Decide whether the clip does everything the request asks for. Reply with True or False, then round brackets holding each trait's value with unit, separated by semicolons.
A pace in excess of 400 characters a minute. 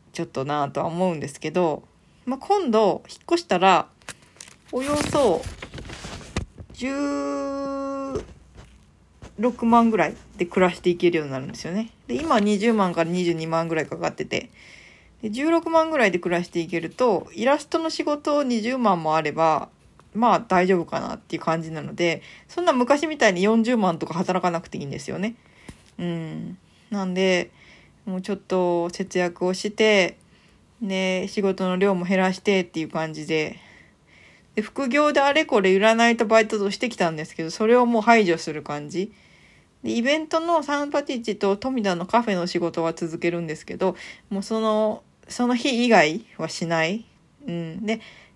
False (310 characters per minute)